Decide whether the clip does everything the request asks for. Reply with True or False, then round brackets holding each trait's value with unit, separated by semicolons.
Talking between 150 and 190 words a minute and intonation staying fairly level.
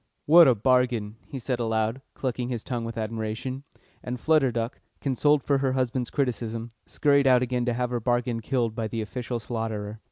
True (185 wpm; 2.3 semitones)